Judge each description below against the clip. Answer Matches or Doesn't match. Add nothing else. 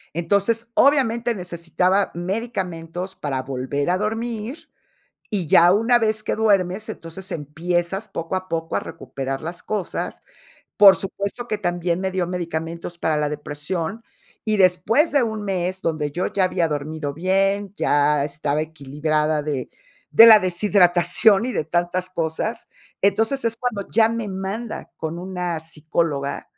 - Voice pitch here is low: Doesn't match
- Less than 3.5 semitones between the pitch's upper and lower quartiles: Doesn't match